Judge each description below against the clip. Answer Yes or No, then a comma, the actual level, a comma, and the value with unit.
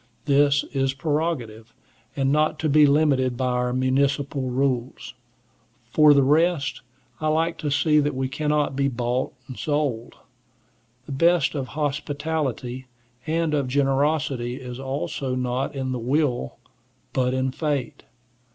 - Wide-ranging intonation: No, average, 2.7 semitones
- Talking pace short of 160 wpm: Yes, slow, 135 wpm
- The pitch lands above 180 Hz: No, medium, 140 Hz